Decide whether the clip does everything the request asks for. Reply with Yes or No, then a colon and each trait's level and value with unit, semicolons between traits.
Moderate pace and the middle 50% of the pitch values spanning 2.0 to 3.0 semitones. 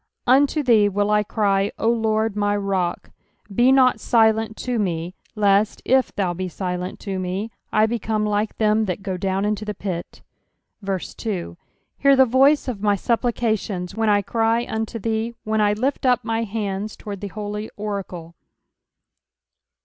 Yes: average, 155 wpm; narrow, 2.4 semitones